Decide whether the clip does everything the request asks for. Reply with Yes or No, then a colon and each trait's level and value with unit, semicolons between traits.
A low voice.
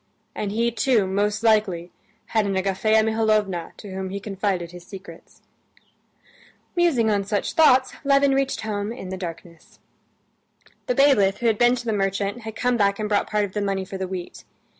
No: high, 205 Hz